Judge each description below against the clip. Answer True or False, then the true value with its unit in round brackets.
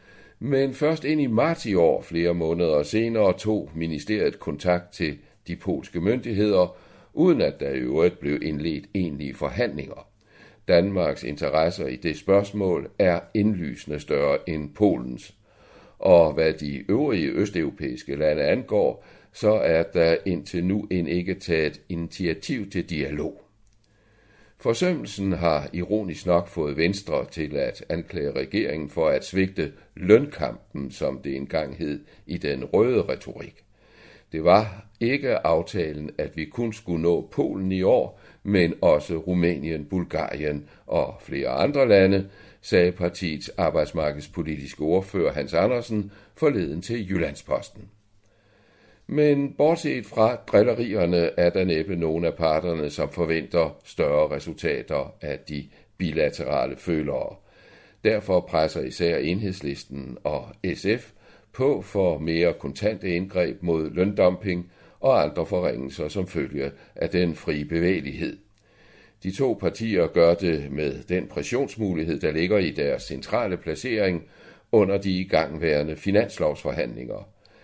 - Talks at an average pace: False (125 wpm)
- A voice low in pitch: True (90 Hz)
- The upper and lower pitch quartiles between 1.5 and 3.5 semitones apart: False (4.4 semitones)